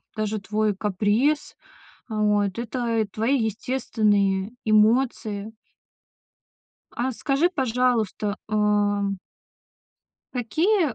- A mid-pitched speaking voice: No, high, 215 Hz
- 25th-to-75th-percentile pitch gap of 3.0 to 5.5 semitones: Yes, average, 3.3 semitones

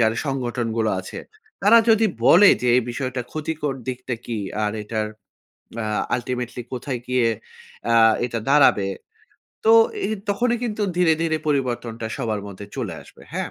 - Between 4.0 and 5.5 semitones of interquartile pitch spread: Yes, average, 5.2 semitones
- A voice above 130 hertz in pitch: No, low, 125 Hz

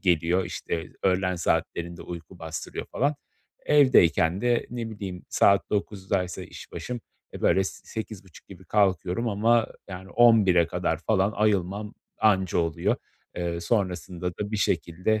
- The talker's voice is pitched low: Yes, very low, 95 Hz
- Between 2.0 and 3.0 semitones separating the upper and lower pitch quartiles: No, average, 3.5 semitones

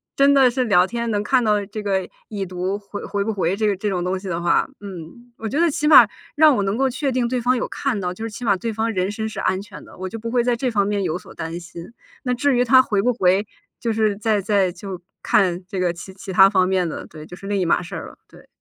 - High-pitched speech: Yes, high, 205 Hz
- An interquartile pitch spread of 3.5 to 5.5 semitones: Yes, average, 4.1 semitones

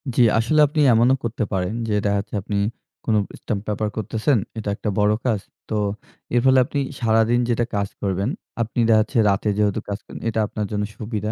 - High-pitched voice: No, low, 110 Hz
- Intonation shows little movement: Yes, narrow, 2.2 semitones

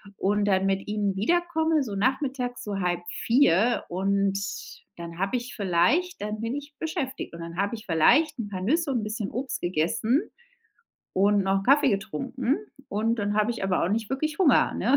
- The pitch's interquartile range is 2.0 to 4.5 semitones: No, wide, 5.4 semitones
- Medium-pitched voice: No, high, 215 Hz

